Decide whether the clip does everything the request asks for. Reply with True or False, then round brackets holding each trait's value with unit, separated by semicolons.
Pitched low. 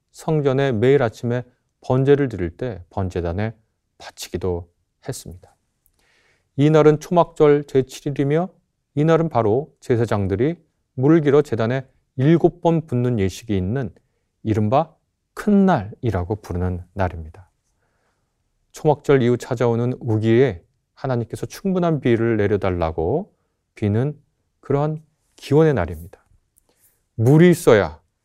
True (125 Hz)